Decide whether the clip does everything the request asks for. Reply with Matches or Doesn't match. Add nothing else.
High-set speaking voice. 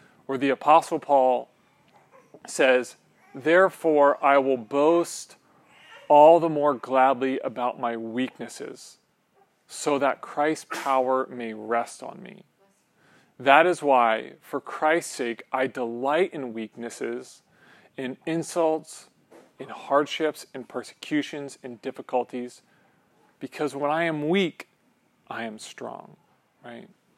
Doesn't match